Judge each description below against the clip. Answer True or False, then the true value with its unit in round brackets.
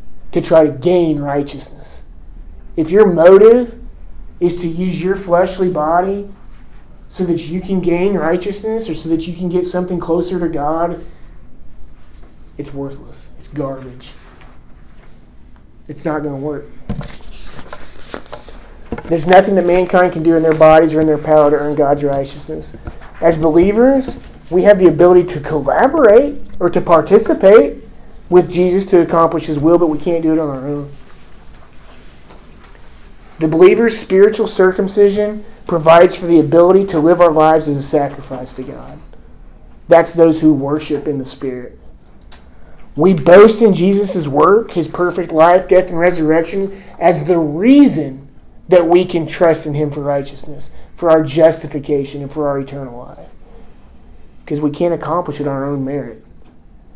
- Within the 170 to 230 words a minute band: False (150 wpm)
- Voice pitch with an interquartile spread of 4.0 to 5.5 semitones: True (4.4 semitones)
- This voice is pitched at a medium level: True (160 Hz)